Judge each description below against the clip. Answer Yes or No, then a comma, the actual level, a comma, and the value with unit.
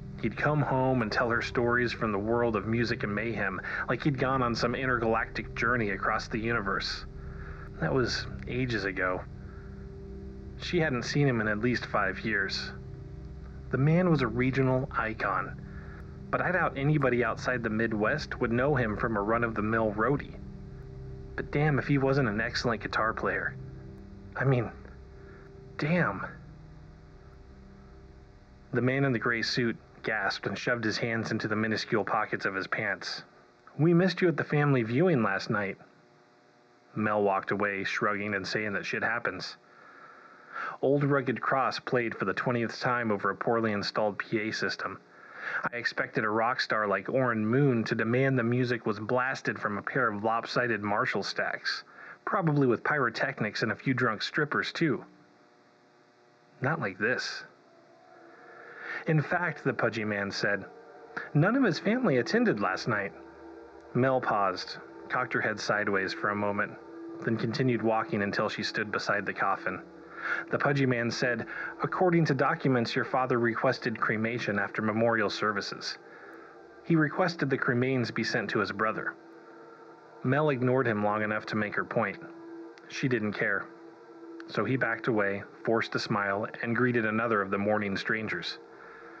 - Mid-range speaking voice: No, low, 115 Hz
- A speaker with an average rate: Yes, average, 155 wpm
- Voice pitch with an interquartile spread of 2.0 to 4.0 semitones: No, average, 4.5 semitones